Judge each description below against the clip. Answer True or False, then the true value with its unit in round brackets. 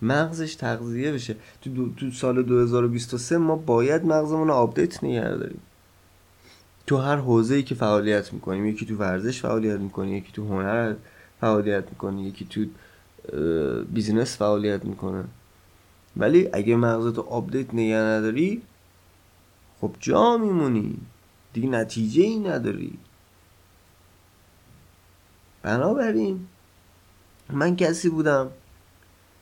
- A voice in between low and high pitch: False (110 Hz)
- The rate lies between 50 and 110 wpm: True (105 wpm)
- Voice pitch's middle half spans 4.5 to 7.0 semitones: True (4.9 semitones)